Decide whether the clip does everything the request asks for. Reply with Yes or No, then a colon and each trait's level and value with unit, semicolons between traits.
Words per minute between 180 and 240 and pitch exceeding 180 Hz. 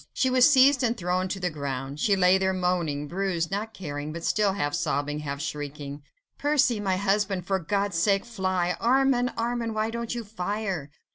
Yes: average, 185 wpm; high, 190 Hz